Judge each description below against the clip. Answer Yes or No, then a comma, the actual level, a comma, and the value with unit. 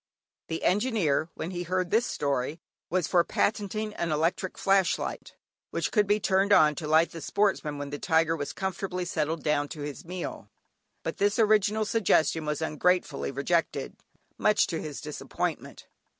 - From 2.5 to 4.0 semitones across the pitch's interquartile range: No, average, 4.4 semitones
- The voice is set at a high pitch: No, medium, 170 Hz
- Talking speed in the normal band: Yes, average, 165 wpm